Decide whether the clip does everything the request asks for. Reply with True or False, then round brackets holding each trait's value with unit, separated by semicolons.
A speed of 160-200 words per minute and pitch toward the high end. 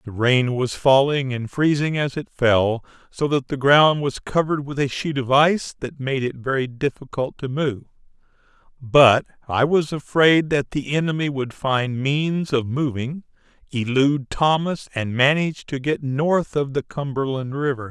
False (170 wpm; 140 Hz)